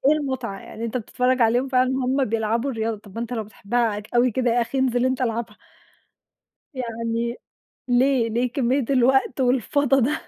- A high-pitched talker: Yes, high, 245 Hz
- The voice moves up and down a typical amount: No, narrow, 2.2 semitones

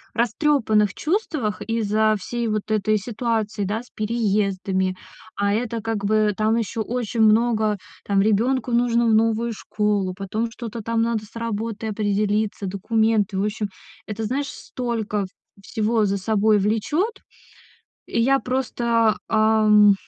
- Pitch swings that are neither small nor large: No, narrow, 1.9 semitones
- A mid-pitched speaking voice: No, high, 220 Hz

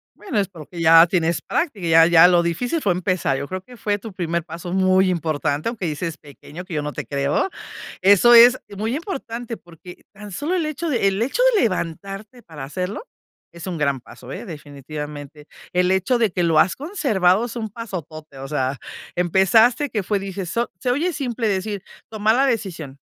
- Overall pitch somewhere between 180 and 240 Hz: Yes, medium, 185 Hz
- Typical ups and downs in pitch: No, wide, 5.9 semitones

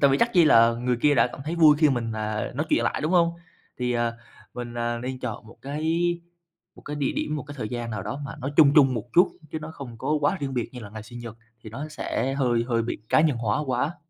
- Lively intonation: No, average, 4.3 semitones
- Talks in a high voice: No, low, 130 Hz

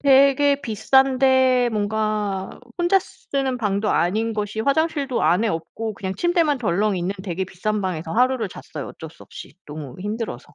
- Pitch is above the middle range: Yes, high, 220 Hz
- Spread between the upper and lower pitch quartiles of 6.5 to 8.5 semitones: No, wide, 5.5 semitones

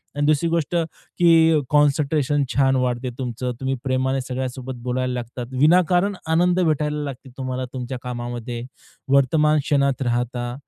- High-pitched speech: No, low, 135 Hz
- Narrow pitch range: No, average, 3.4 semitones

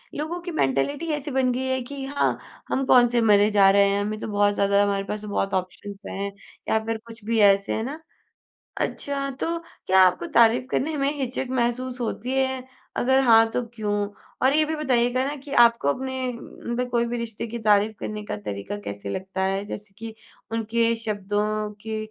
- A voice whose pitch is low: No, high, 225 Hz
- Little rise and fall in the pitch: No, average, 4.3 semitones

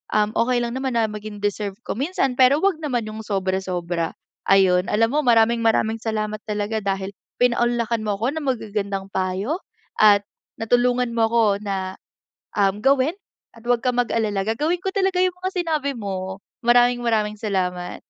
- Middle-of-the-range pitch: No, high, 220 Hz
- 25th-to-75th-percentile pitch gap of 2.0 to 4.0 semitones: Yes, average, 3.6 semitones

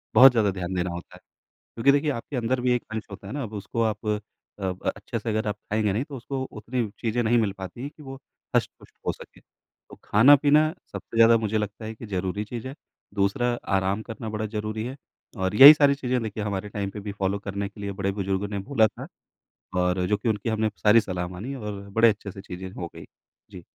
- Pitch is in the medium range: No, low, 110 Hz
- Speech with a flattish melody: No, average, 3.3 semitones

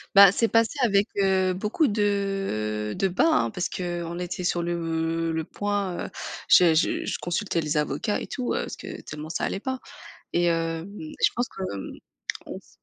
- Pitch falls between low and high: Yes, medium, 180 Hz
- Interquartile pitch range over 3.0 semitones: Yes, average, 3.7 semitones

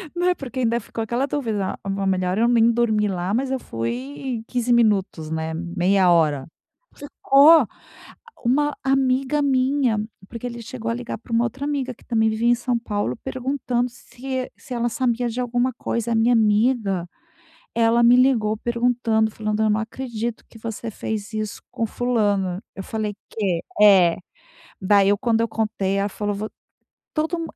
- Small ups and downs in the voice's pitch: No, average, 3.3 semitones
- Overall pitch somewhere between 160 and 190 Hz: No, high, 230 Hz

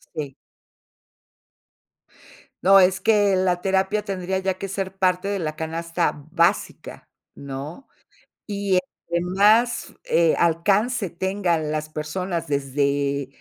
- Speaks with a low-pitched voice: No, medium, 180 Hz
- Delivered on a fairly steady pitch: No, average, 3.7 semitones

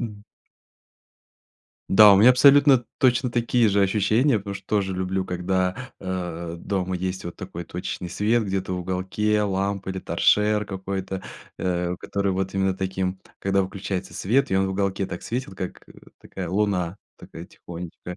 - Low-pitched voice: Yes, very low, 95 Hz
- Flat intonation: Yes, narrow, 2.2 semitones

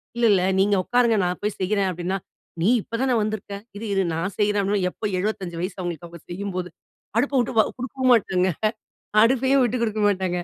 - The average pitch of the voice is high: Yes, high, 205 Hz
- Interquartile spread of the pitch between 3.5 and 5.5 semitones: Yes, average, 3.8 semitones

